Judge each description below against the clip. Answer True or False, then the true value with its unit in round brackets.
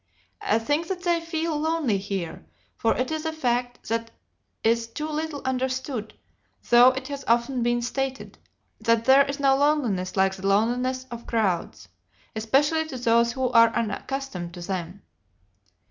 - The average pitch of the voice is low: False (245 Hz)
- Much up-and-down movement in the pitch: False (3.8 semitones)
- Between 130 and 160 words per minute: True (155 wpm)